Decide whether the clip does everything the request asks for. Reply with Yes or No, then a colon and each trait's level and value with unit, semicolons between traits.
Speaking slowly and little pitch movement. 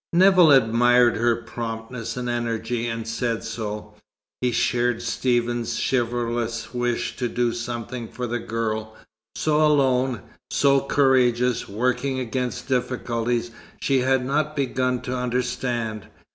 Yes: slow, 120 wpm; narrow, 1.8 semitones